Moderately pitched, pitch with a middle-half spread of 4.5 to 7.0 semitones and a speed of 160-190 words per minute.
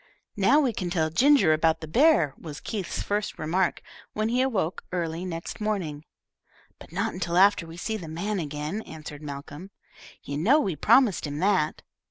Yes: medium, 175 Hz; average, 5.1 semitones; average, 180 wpm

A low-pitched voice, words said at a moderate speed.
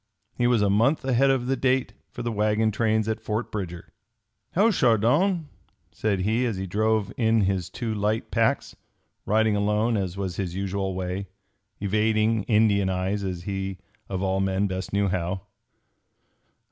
Yes: low, 105 Hz; average, 160 wpm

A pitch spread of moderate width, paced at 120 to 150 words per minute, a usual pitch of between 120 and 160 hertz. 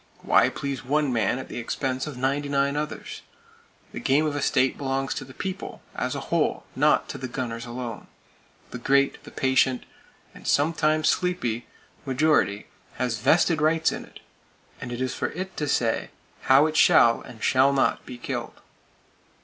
No: average, 3.2 semitones; average, 165 wpm; low, 135 Hz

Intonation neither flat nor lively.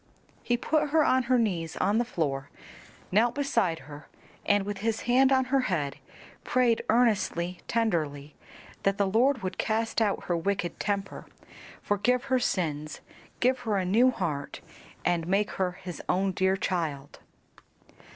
No: wide, 5.7 semitones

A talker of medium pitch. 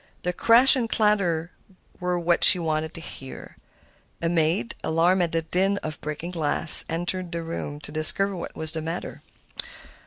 Yes: medium, 170 Hz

